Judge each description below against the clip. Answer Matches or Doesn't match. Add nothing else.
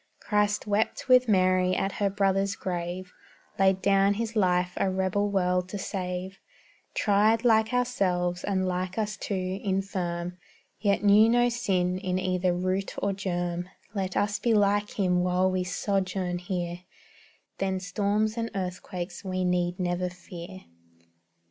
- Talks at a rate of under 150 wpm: Matches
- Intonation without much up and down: Matches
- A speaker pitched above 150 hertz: Matches